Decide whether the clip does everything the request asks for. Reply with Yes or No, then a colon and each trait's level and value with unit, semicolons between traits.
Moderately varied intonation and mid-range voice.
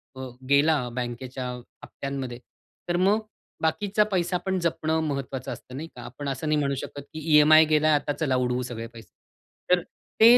Yes: average, 4.0 semitones; medium, 145 Hz